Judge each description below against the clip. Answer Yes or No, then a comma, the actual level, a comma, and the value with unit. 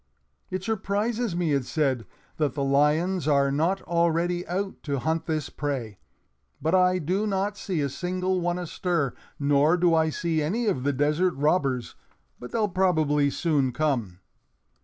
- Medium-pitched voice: Yes, medium, 160 Hz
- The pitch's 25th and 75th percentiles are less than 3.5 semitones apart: No, average, 4.4 semitones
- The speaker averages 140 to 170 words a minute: Yes, average, 160 wpm